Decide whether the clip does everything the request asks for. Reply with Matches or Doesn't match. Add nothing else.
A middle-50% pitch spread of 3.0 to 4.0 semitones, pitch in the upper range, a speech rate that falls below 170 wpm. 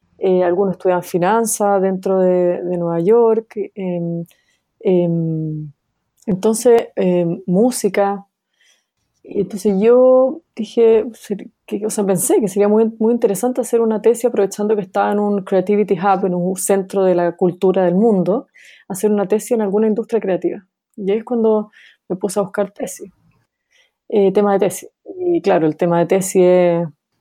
Matches